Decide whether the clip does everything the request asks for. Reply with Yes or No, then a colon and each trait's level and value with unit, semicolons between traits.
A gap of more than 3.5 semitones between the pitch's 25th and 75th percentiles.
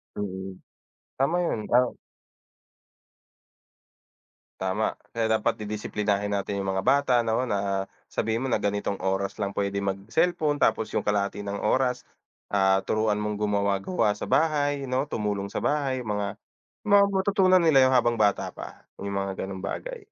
Yes: average, 4.7 semitones